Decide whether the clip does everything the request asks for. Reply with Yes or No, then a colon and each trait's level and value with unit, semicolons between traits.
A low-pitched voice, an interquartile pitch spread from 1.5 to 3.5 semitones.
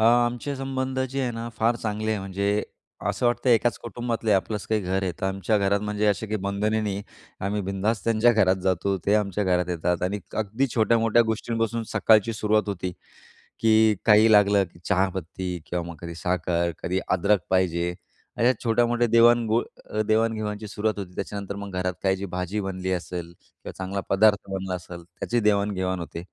Yes: low, 105 Hz; average, 3.1 semitones